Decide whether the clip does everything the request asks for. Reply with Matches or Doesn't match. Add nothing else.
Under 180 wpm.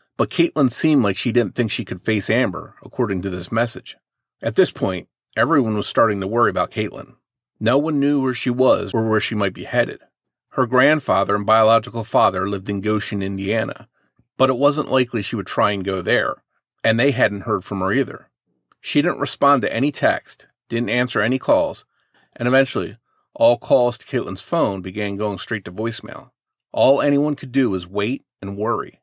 Doesn't match